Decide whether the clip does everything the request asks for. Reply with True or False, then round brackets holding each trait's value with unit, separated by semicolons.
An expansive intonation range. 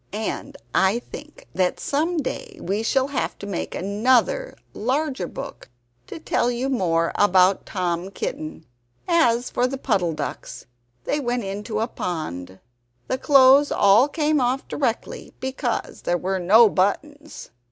True (6.4 semitones)